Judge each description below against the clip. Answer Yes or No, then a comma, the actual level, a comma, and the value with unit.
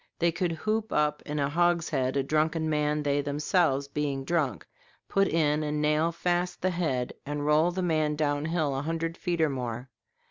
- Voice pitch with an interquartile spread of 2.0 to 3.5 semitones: Yes, average, 2.7 semitones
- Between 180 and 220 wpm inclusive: Yes, average, 185 wpm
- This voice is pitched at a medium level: Yes, medium, 150 Hz